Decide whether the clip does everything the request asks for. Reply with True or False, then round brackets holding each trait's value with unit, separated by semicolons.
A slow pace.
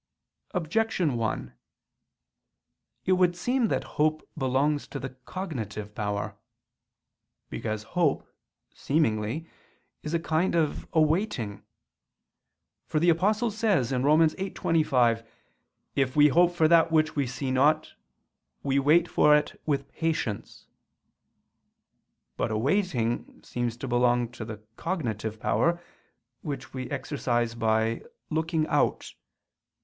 True (115 wpm)